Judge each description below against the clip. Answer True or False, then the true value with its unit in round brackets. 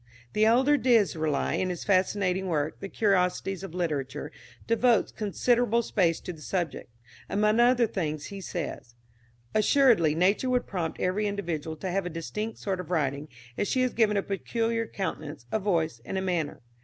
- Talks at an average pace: True (170 wpm)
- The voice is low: False (190 Hz)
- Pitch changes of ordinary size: True (4.8 semitones)